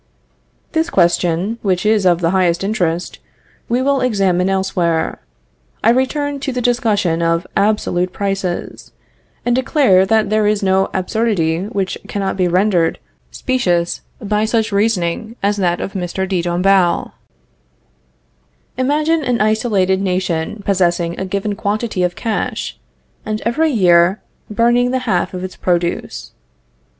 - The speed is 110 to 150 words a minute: Yes, slow, 135 wpm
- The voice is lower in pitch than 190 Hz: No, high, 195 Hz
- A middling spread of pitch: Yes, average, 4.0 semitones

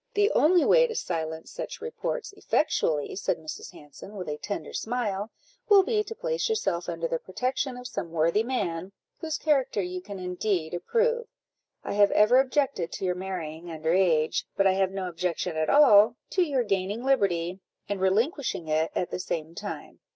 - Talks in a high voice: Yes, high, 195 Hz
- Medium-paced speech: Yes, average, 180 wpm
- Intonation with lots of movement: Yes, wide, 7.7 semitones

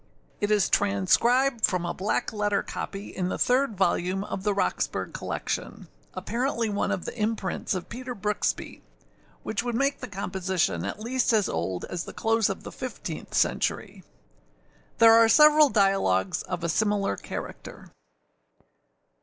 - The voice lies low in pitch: No, high, 205 Hz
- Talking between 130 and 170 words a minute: Yes, average, 150 wpm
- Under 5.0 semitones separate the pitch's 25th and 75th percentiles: Yes, average, 3.7 semitones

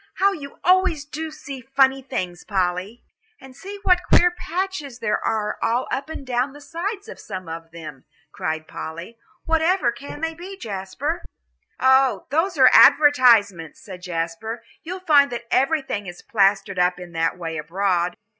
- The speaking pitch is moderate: No, very high, 250 Hz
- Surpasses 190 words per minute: No, average, 165 wpm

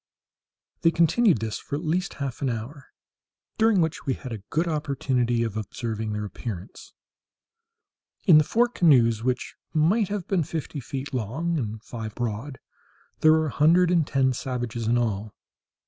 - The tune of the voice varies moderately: No, wide, 5.9 semitones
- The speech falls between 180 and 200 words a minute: No, average, 160 wpm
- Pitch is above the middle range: No, low, 135 Hz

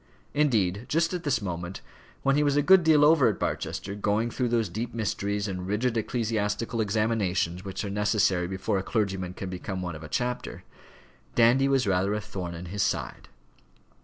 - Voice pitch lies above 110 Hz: No, low, 105 Hz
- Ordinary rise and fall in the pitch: Yes, average, 4.4 semitones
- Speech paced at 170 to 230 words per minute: Yes, average, 185 wpm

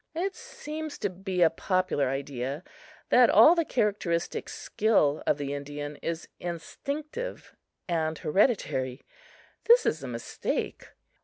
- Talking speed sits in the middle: No, slow, 125 wpm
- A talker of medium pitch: Yes, medium, 175 Hz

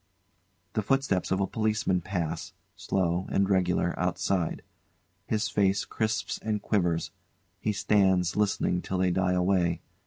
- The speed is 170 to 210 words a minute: No, slow, 135 wpm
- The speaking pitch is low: Yes, very low, 95 Hz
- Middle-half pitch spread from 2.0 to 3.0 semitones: Yes, narrow, 2.4 semitones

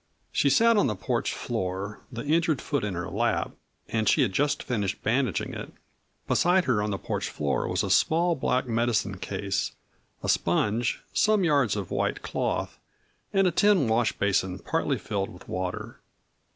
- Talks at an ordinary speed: Yes, average, 170 wpm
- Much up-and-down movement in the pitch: Yes, wide, 7.2 semitones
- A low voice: Yes, low, 115 Hz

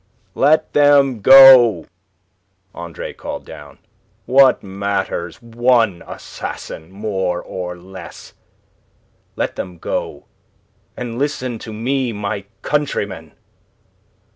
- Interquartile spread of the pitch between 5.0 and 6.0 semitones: Yes, wide, 5.5 semitones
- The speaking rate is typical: No, slow, 95 wpm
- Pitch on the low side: Yes, low, 110 Hz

